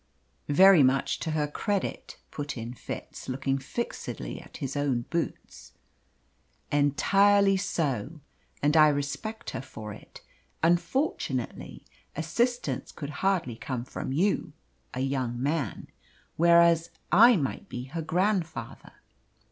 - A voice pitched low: No, medium, 150 Hz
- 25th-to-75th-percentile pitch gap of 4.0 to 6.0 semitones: Yes, average, 5.1 semitones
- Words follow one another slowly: Yes, slow, 115 wpm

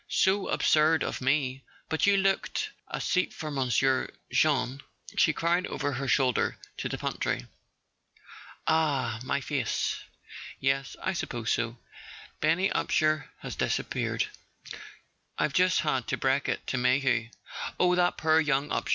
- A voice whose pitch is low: No, medium, 145 Hz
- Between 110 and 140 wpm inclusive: Yes, slow, 135 wpm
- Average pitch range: Yes, average, 3.7 semitones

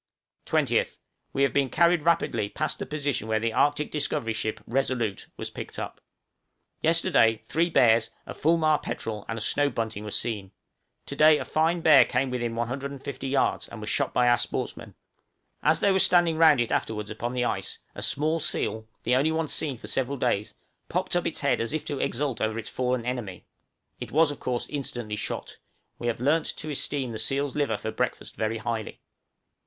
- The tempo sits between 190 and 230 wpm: Yes, average, 195 wpm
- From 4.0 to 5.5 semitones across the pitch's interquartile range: Yes, average, 4.8 semitones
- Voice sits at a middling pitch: No, low, 130 Hz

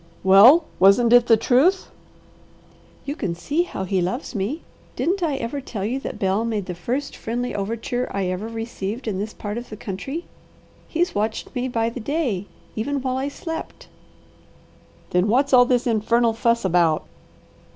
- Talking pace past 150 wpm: Yes, average, 170 wpm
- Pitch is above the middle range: Yes, high, 230 Hz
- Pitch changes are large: No, average, 4.6 semitones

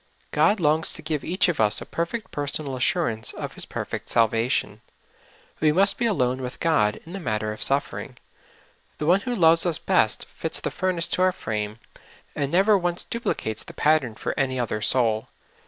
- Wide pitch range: Yes, wide, 7.1 semitones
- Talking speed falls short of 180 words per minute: No, average, 190 wpm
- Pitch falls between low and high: Yes, medium, 150 Hz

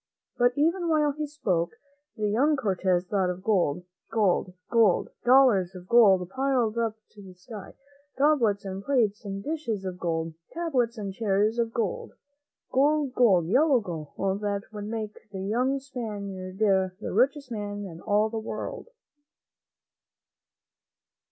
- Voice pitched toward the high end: Yes, high, 215 Hz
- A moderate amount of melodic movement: Yes, average, 4.8 semitones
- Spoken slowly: No, average, 145 wpm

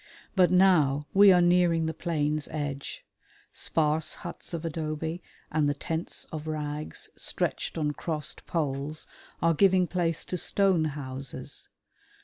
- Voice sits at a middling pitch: Yes, medium, 160 Hz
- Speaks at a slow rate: Yes, slow, 130 wpm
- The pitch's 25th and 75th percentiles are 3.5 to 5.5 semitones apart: No, average, 2.8 semitones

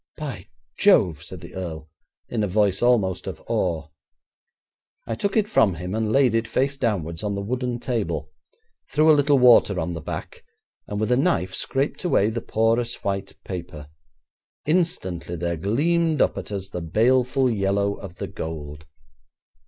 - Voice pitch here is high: No, low, 105 Hz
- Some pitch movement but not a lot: No, wide, 6.1 semitones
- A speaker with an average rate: Yes, average, 165 wpm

